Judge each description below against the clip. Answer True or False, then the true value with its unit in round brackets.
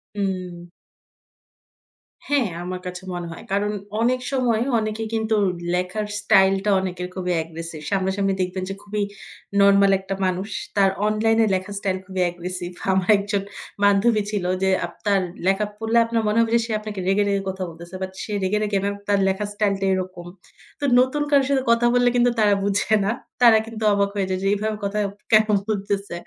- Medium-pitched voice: False (200 Hz)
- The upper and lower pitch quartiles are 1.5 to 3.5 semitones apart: True (2.5 semitones)